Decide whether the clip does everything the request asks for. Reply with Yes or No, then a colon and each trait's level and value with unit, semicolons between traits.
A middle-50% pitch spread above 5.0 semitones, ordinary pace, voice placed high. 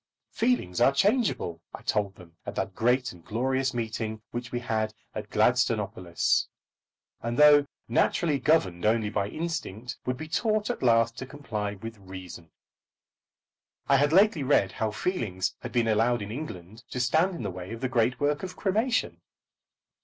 No: wide, 5.6 semitones; average, 165 wpm; low, 120 Hz